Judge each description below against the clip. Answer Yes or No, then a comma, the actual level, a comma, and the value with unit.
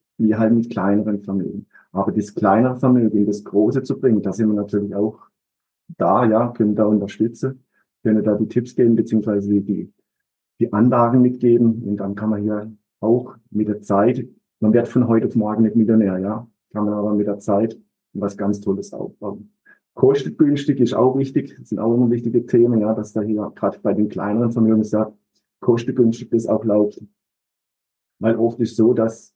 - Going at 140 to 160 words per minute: No, average, 180 wpm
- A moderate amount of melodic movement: No, narrow, 2.2 semitones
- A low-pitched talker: Yes, low, 110 Hz